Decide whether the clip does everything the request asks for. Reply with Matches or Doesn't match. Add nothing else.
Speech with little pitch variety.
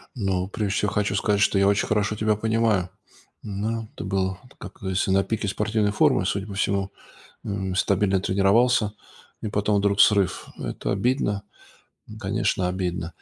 Matches